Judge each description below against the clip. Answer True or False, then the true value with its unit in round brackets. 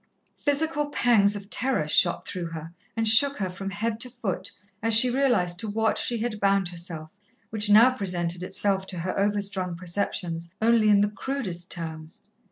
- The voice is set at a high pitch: True (200 Hz)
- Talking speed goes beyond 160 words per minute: True (175 wpm)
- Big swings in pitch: False (4.2 semitones)